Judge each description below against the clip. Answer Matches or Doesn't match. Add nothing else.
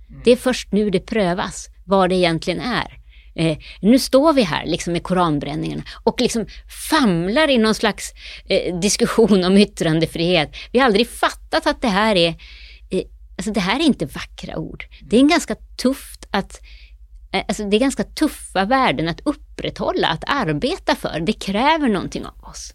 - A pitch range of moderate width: Doesn't match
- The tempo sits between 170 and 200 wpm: Matches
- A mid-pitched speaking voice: Doesn't match